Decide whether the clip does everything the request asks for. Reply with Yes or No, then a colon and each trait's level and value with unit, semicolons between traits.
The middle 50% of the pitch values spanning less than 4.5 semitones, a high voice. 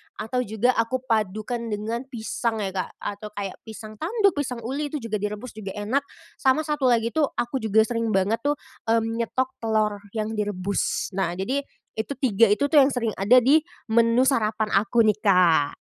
Yes: average, 3.5 semitones; high, 225 Hz